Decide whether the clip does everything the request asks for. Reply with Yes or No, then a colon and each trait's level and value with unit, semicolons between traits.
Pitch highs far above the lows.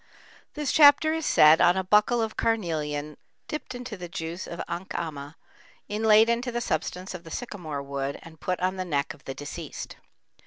Yes: wide, 6.4 semitones